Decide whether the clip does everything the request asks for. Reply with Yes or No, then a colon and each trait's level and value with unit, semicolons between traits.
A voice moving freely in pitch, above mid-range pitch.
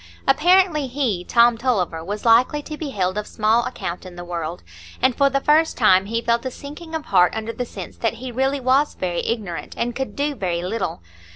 Yes: wide, 6.5 semitones; high, 235 Hz